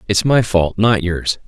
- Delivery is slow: No, fast, 205 wpm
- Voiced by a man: Yes, male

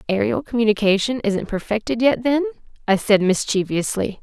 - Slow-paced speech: Yes, slow, 130 wpm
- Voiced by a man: No, female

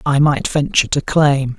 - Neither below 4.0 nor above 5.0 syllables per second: Yes, 4.8 syllables/s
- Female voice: No, male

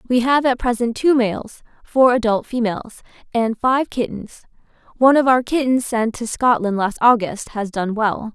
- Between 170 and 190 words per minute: Yes, average, 175 wpm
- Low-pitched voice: No, high, 235 Hz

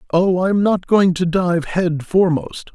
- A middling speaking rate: Yes, average, 195 wpm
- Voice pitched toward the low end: No, medium, 175 Hz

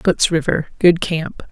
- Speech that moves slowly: Yes, slow, 120 wpm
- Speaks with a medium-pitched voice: Yes, medium, 165 Hz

